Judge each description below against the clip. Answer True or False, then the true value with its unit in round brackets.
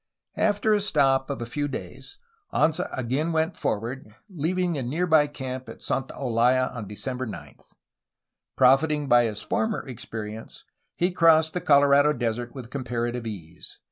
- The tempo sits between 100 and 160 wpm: True (150 wpm)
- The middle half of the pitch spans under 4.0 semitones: False (4.7 semitones)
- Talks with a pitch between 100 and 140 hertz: True (135 Hz)